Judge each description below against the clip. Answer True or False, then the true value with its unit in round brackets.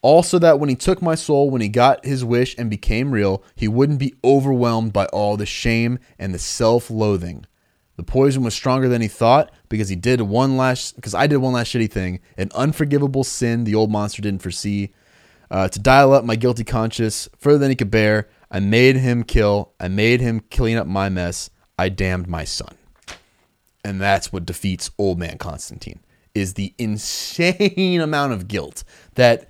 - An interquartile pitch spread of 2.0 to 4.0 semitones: False (4.5 semitones)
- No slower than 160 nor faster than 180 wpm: False (190 wpm)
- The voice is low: True (115 Hz)